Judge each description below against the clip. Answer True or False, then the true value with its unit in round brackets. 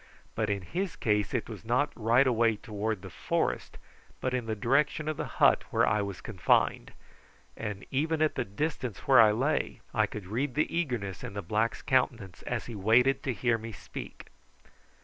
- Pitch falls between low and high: False (115 Hz)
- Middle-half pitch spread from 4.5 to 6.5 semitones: False (3.9 semitones)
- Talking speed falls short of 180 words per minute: False (190 wpm)